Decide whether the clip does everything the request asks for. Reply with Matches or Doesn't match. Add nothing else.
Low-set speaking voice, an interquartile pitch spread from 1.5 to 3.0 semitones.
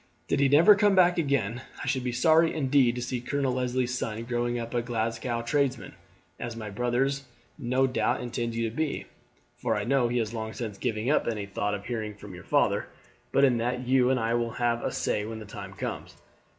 Matches